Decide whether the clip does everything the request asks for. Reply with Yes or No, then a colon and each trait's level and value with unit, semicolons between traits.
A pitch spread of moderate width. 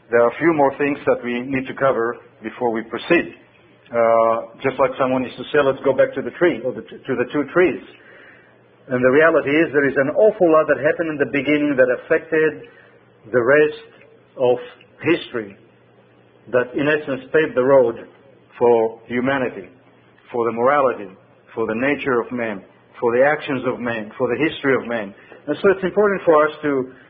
Yes: average, 4.1 semitones